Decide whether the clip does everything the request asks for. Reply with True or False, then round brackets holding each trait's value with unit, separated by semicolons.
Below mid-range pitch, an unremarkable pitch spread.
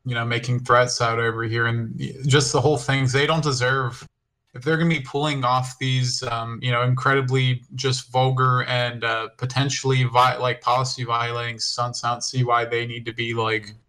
False (125 Hz; 1.9 semitones)